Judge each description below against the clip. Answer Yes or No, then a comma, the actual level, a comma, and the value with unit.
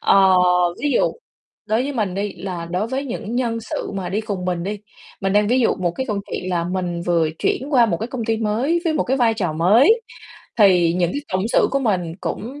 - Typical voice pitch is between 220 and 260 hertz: No, high, 210 Hz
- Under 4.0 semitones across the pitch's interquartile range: No, average, 4.9 semitones